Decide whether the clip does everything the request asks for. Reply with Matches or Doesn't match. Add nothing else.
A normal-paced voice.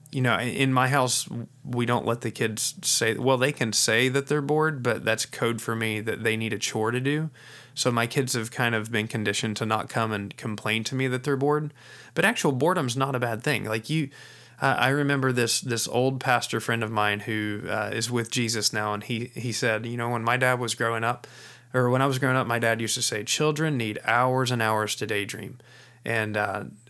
Doesn't match